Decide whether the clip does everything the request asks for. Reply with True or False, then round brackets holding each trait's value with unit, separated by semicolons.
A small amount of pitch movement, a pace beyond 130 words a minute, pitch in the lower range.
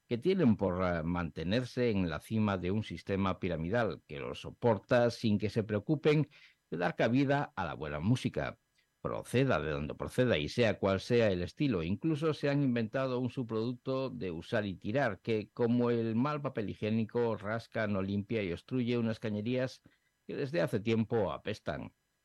False (4.0 semitones; 170 wpm; 115 Hz)